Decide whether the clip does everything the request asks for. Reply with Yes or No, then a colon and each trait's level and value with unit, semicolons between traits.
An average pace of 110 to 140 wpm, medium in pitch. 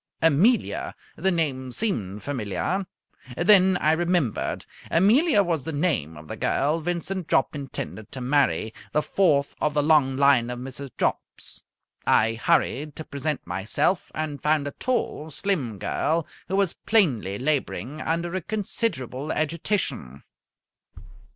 Yes: slow, 135 wpm; medium, 150 Hz